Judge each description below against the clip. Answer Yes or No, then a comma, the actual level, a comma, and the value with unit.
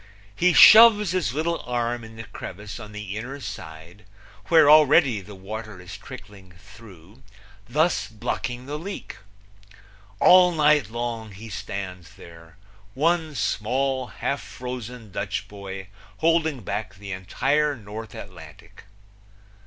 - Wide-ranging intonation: Yes, wide, 6.6 semitones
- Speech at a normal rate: No, slow, 125 wpm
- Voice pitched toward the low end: Yes, low, 115 Hz